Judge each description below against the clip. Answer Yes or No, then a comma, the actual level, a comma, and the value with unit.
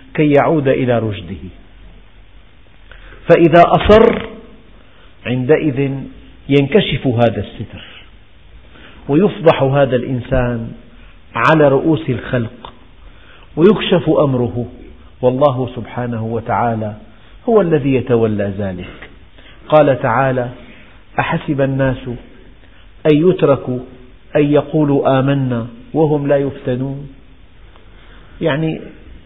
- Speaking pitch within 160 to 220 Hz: No, low, 125 Hz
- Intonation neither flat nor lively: Yes, average, 5.0 semitones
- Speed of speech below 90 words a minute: Yes, average, 80 wpm